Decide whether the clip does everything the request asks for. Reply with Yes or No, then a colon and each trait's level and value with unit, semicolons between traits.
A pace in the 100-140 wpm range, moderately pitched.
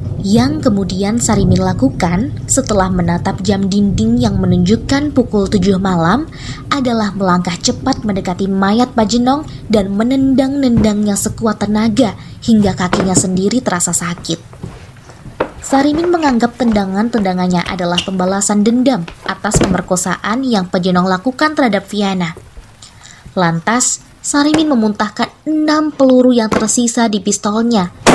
No: average, 105 wpm; high, 210 Hz